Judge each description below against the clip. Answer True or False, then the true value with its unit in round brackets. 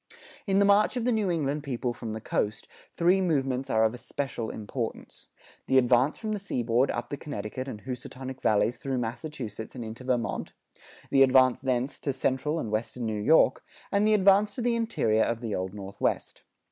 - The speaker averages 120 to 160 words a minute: False (185 wpm)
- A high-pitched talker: False (130 Hz)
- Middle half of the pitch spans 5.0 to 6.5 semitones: True (5.6 semitones)